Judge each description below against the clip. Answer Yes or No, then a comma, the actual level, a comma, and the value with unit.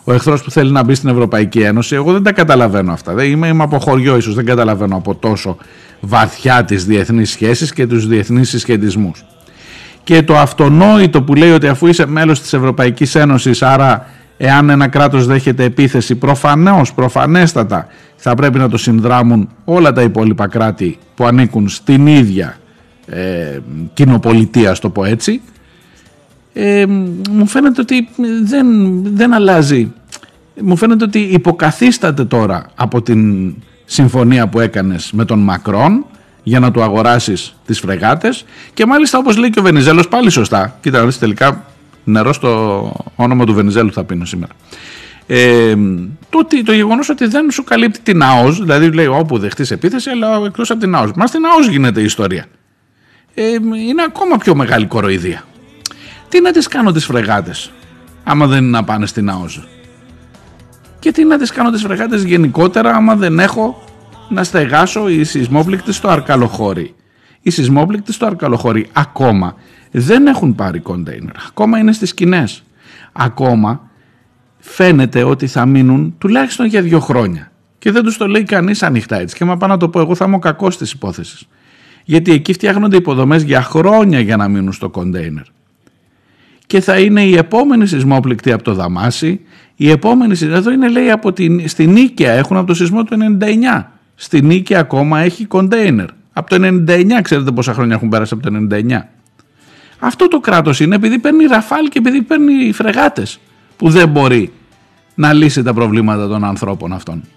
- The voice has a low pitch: No, medium, 145 Hz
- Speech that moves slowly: No, average, 165 wpm